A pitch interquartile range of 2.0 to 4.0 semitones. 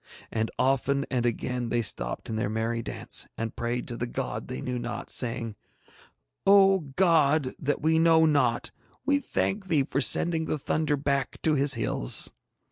No: average, 5.2 semitones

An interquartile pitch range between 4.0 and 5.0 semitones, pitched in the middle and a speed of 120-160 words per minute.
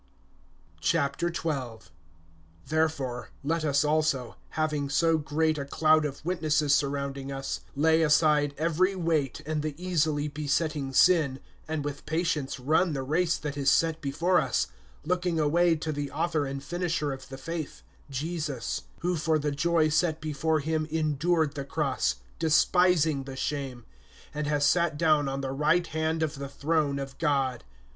No: narrow, 2.5 semitones; medium, 150 Hz; average, 150 wpm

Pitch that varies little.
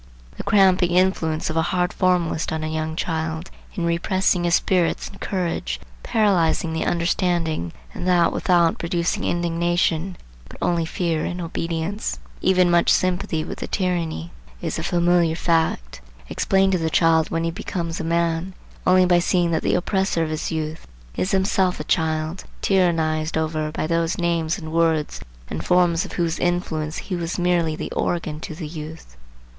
Yes: narrow, 2.0 semitones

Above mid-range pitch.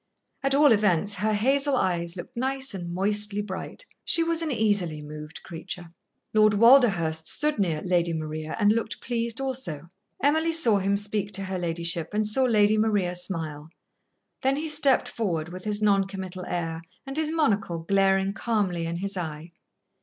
Yes: high, 200 Hz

